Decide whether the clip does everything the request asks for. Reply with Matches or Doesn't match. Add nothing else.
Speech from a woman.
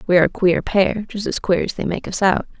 Matches